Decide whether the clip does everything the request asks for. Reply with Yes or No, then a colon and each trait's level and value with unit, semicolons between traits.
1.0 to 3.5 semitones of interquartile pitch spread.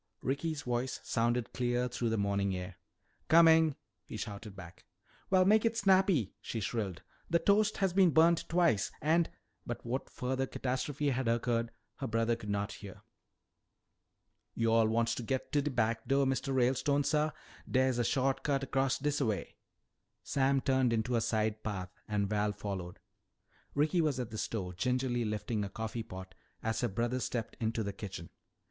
No: average, 4.4 semitones